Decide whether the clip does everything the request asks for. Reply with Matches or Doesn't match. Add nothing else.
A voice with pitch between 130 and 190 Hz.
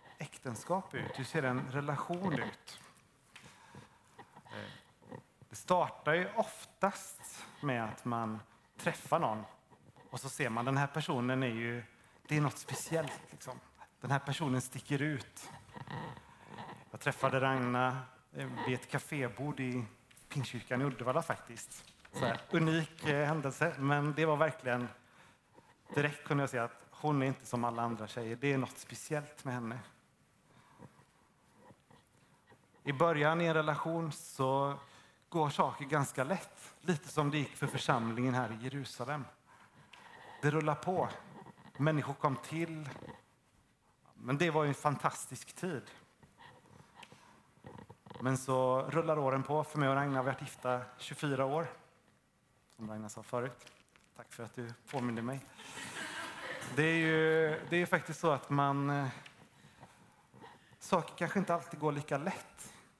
Matches